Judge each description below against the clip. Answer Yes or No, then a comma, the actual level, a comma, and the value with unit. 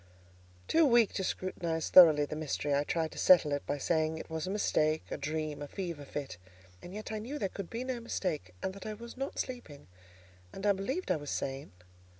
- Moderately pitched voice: Yes, medium, 170 Hz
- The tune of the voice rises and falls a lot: Yes, wide, 5.9 semitones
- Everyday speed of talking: No, fast, 215 wpm